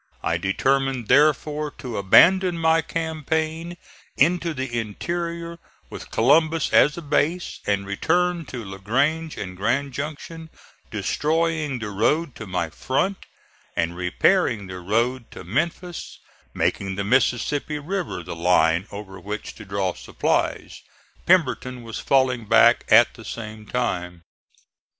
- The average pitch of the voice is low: Yes, low, 130 Hz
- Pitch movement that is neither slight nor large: No, wide, 7.9 semitones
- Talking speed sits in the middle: No, slow, 130 wpm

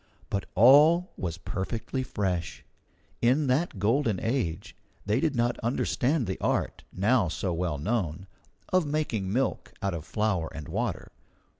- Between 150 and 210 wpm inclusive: No, average, 140 wpm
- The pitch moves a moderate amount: No, wide, 6.0 semitones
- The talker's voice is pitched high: No, low, 110 Hz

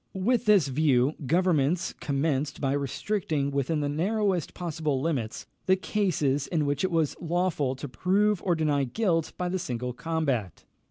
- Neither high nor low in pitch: Yes, medium, 155 Hz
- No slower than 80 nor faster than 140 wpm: No, average, 155 wpm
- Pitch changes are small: No, average, 4.6 semitones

